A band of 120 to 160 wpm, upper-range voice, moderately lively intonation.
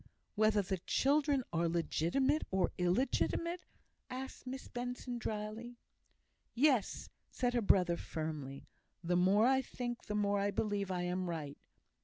No: slow, 135 wpm; high, 210 Hz; wide, 5.9 semitones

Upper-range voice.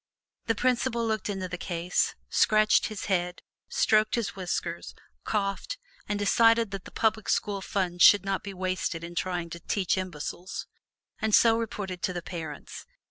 Yes: high, 195 Hz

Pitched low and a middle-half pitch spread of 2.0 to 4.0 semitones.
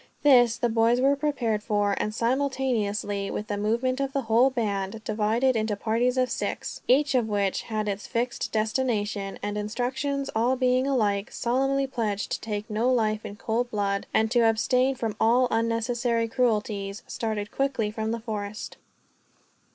No: high, 225 Hz; average, 3.1 semitones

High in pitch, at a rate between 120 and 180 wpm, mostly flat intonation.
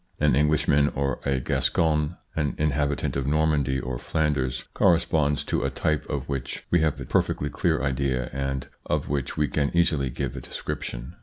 No: very low, 70 Hz; average, 170 wpm; narrow, 2.1 semitones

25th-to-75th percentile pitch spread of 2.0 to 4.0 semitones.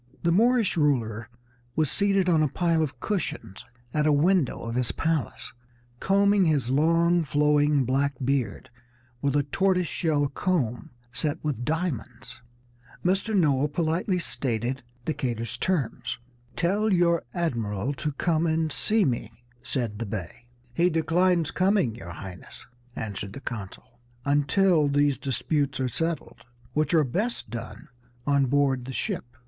No: average, 5.2 semitones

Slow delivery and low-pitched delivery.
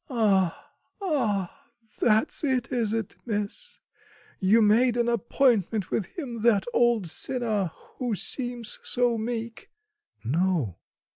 No: slow, 115 wpm; high, 225 Hz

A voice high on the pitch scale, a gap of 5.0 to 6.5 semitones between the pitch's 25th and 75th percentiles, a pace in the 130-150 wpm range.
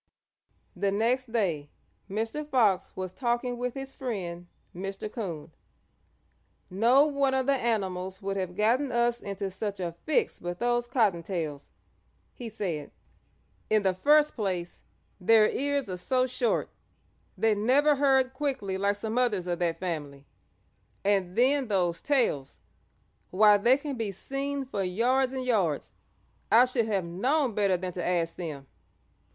Yes: high, 215 Hz; wide, 5.6 semitones; average, 145 wpm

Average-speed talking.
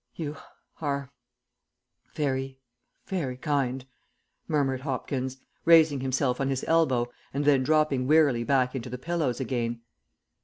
No: slow, 120 wpm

